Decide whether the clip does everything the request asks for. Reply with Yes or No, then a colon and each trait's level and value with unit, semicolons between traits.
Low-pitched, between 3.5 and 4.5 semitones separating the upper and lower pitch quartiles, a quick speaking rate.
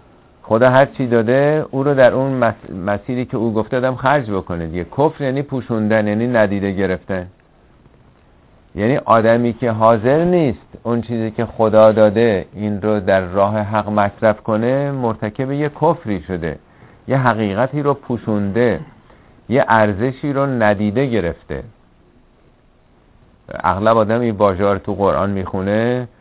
No: low, 115 Hz; average, 3.9 semitones; average, 135 wpm